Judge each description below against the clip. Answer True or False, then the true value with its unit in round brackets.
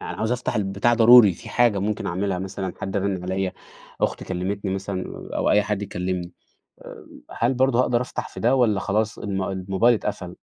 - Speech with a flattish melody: False (3.3 semitones)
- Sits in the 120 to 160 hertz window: False (100 Hz)